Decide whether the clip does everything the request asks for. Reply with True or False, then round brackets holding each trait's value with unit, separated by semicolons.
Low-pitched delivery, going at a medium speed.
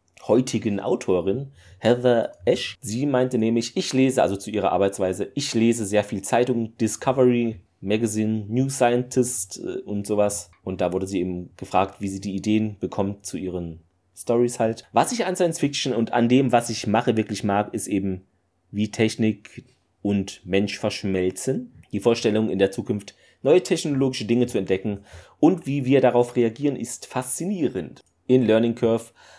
True (110 Hz; 160 wpm)